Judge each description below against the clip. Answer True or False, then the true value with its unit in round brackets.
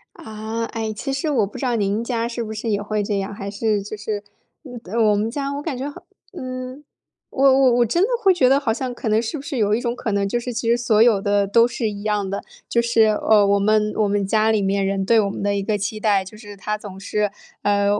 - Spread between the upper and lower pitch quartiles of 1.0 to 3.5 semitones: True (2.8 semitones)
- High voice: True (215 Hz)